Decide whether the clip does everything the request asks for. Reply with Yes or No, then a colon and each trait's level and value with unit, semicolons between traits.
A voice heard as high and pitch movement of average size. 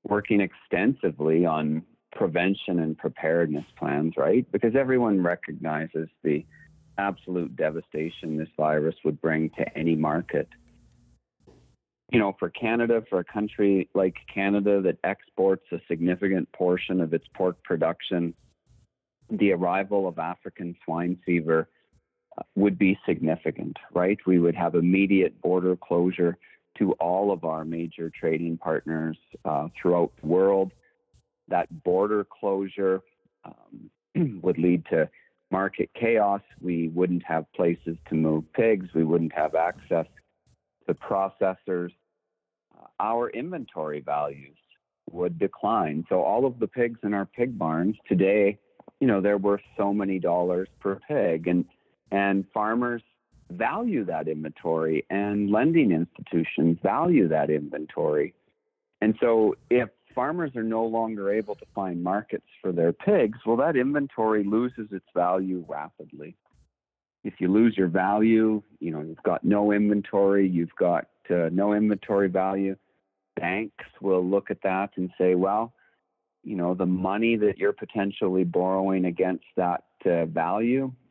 No: very low, 95 Hz; average, 3.6 semitones